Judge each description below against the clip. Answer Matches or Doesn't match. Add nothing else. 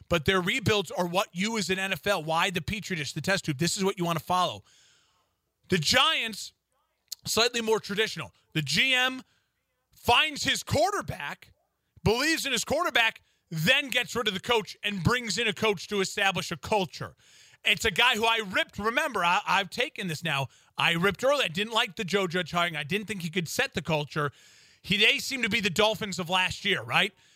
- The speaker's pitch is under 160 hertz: Doesn't match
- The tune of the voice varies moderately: Matches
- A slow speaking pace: Doesn't match